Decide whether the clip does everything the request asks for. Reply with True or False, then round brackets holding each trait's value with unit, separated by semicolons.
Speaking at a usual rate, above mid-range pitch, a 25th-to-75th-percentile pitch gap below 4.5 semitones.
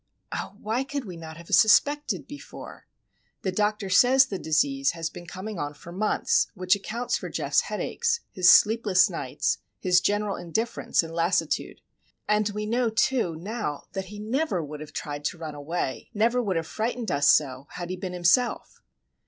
False (170 wpm; 195 Hz; 5.5 semitones)